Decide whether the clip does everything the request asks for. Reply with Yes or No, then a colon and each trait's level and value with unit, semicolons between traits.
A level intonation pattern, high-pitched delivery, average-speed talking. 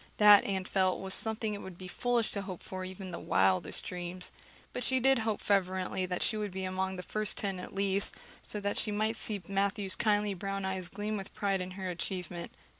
No: narrow, 2.1 semitones; high, 195 Hz; fast, 220 wpm